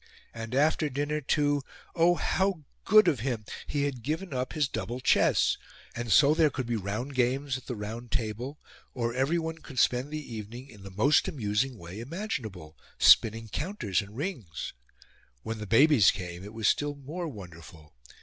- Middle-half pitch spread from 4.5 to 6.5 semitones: Yes, wide, 5.5 semitones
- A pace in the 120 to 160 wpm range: No, average, 170 wpm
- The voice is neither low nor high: No, low, 125 Hz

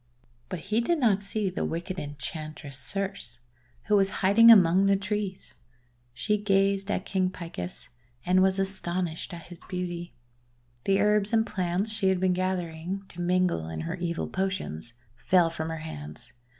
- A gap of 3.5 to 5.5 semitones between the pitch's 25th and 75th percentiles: No, average, 3.0 semitones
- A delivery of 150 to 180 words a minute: Yes, average, 160 wpm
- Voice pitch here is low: No, medium, 185 Hz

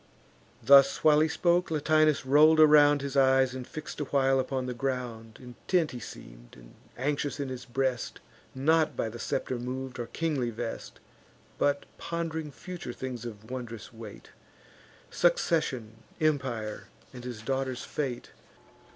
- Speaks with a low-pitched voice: Yes, low, 130 Hz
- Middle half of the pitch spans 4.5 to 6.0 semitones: No, average, 3.7 semitones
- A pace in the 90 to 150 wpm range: Yes, average, 140 wpm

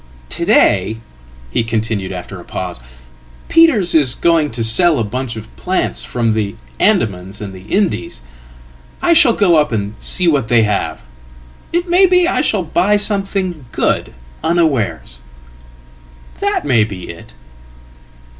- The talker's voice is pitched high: No, low, 130 Hz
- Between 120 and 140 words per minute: Yes, slow, 135 wpm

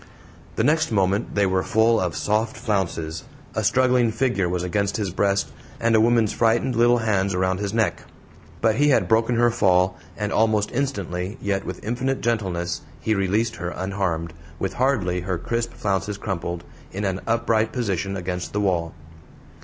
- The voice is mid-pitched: No, low, 100 Hz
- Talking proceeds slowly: No, average, 170 wpm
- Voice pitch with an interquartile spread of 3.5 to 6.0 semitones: Yes, average, 3.8 semitones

